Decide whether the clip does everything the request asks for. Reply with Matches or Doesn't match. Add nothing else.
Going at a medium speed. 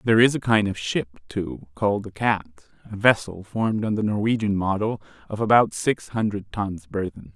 Matches